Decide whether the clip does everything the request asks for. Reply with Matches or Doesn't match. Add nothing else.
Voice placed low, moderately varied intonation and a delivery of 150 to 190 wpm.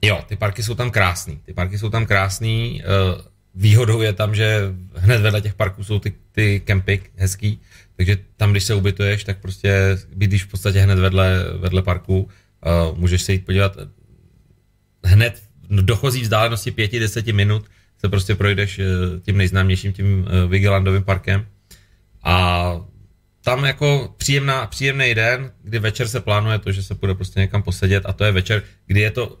Doesn't match